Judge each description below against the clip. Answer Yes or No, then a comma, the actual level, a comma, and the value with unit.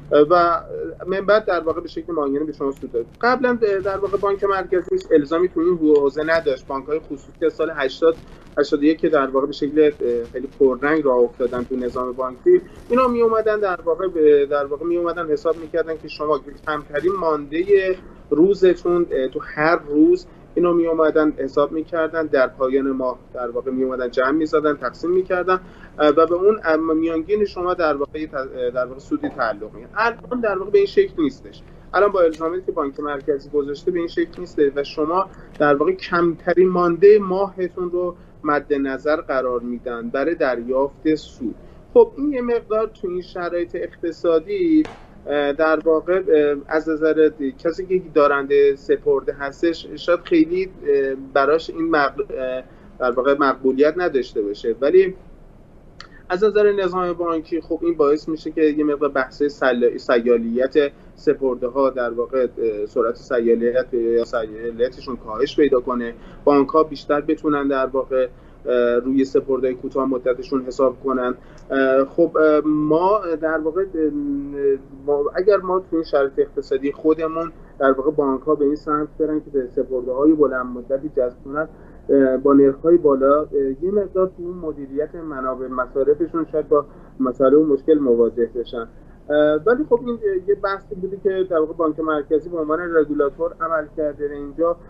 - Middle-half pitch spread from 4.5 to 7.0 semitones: Yes, average, 4.9 semitones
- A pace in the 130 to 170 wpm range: Yes, fast, 155 wpm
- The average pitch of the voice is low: No, medium, 155 Hz